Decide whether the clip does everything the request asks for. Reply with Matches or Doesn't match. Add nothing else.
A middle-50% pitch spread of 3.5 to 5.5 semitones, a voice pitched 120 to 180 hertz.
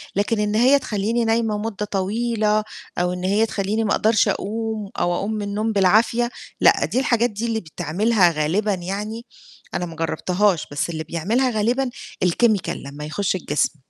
Doesn't match